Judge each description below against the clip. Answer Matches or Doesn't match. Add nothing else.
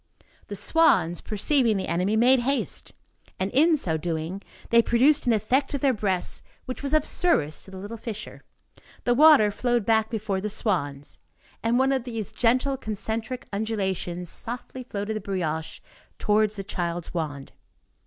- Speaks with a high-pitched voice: Matches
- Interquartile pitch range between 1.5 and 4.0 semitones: Doesn't match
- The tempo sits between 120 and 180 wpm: Matches